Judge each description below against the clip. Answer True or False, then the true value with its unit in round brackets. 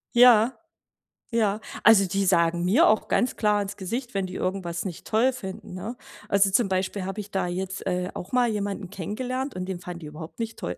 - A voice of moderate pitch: False (195 Hz)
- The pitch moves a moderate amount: True (3.5 semitones)